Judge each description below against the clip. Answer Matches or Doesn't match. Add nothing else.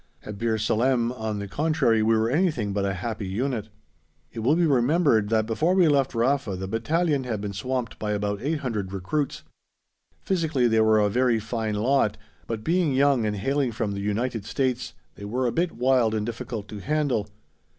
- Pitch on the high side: Doesn't match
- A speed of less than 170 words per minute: Doesn't match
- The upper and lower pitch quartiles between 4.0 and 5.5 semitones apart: Matches